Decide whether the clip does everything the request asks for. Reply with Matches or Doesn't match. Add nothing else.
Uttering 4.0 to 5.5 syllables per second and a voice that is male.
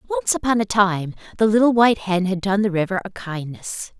Doesn't match